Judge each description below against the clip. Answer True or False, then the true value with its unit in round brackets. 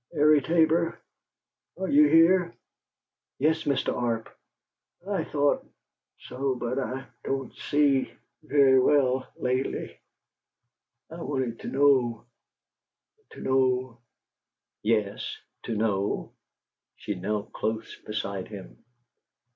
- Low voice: True (130 Hz)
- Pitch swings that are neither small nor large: True (4.3 semitones)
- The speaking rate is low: True (105 wpm)